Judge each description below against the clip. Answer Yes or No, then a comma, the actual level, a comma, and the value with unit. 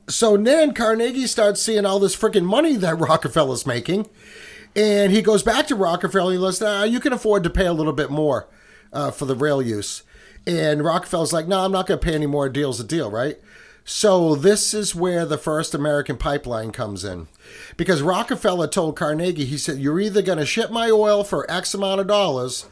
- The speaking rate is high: Yes, fast, 215 wpm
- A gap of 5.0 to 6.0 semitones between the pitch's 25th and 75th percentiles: Yes, wide, 5.5 semitones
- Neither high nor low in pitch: Yes, medium, 180 Hz